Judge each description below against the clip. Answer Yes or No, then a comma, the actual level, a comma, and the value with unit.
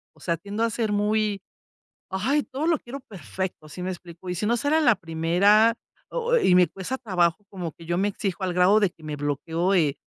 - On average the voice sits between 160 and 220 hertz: Yes, high, 190 Hz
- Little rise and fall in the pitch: No, average, 4.4 semitones